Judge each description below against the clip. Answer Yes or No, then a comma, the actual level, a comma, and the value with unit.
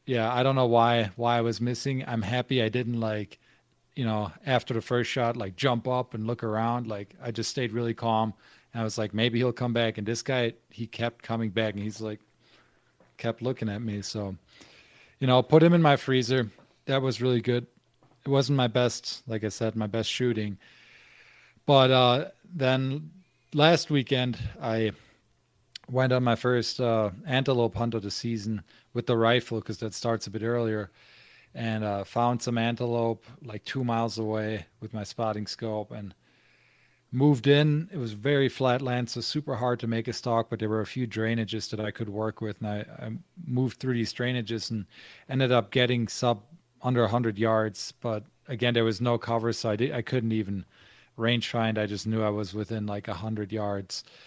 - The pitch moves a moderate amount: No, narrow, 2.3 semitones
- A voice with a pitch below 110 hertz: No, low, 115 Hz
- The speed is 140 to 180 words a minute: No, average, 200 wpm